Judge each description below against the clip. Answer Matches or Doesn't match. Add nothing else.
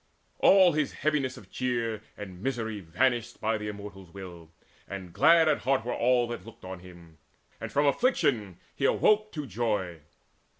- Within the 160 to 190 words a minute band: Matches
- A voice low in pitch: Matches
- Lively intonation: Matches